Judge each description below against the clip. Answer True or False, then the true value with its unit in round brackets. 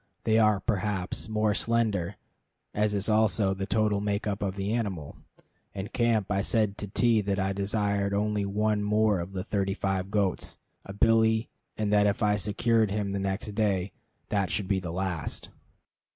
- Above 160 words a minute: True (175 wpm)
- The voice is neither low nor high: False (100 Hz)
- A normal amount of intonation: False (1.7 semitones)